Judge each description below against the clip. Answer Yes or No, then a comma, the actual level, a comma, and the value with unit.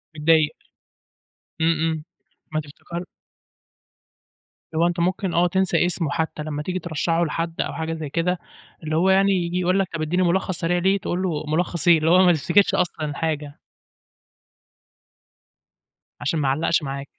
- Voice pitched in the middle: Yes, medium, 165 Hz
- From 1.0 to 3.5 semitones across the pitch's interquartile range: Yes, narrow, 2.4 semitones